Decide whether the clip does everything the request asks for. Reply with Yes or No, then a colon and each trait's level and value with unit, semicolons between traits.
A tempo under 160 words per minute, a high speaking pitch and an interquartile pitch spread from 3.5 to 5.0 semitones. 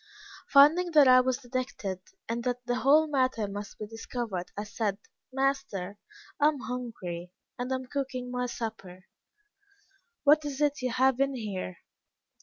Yes: average, 150 wpm; very high, 250 Hz; average, 4.3 semitones